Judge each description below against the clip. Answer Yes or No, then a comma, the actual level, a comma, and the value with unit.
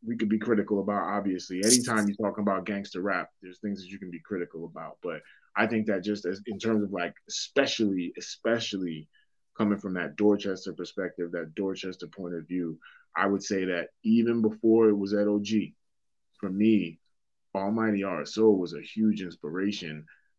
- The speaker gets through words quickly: No, average, 175 wpm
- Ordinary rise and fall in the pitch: Yes, average, 3.1 semitones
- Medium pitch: No, low, 100 Hz